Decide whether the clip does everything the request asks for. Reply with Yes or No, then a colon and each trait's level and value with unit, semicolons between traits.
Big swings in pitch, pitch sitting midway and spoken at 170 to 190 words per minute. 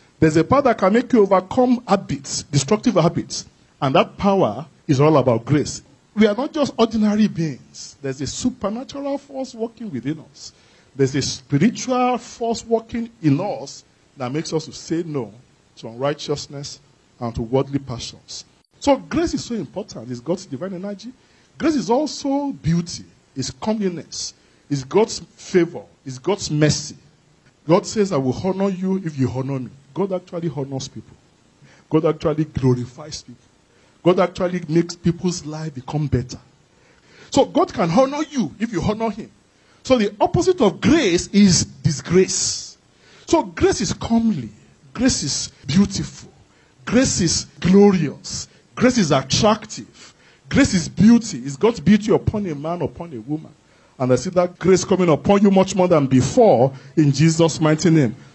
No: wide, 7.5 semitones; medium, 170 Hz; average, 155 wpm